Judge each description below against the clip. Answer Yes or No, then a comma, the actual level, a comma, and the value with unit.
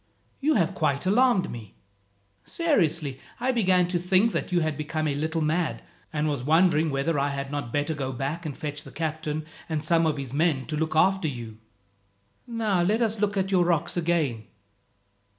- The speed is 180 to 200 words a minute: Yes, average, 185 wpm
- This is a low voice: No, medium, 160 Hz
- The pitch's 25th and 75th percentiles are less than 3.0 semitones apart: No, average, 4.1 semitones